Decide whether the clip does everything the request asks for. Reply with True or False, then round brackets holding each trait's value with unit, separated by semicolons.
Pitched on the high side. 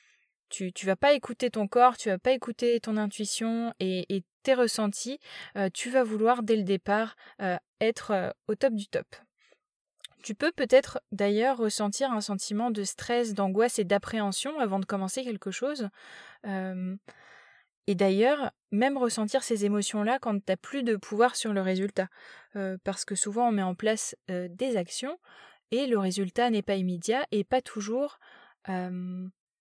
True (215 Hz)